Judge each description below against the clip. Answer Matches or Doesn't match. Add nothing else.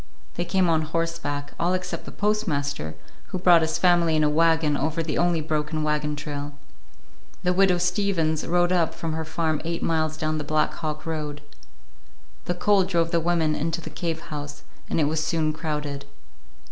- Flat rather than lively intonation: Matches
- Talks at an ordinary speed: Matches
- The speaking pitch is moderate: Matches